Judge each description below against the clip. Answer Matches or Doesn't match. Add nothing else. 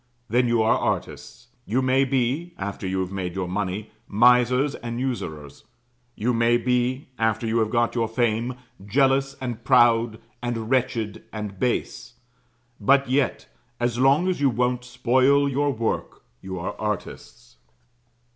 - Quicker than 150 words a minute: Doesn't match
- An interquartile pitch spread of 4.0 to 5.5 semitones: Doesn't match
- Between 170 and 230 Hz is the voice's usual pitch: Doesn't match